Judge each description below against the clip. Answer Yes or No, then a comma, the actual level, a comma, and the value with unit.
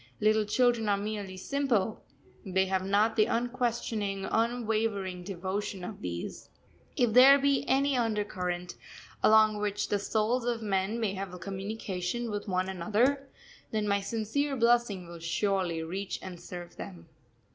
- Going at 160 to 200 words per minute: No, average, 140 wpm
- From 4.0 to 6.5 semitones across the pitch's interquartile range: No, average, 3.4 semitones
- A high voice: Yes, high, 210 Hz